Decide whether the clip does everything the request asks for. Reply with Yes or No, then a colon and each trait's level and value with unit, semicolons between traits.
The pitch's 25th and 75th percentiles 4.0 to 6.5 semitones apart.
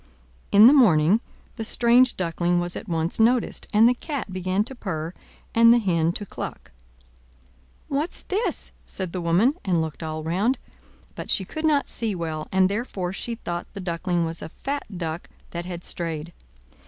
Yes: wide, 5.6 semitones